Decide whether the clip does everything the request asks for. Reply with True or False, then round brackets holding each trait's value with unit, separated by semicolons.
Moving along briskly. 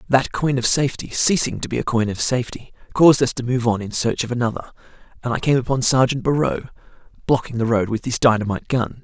True (220 wpm)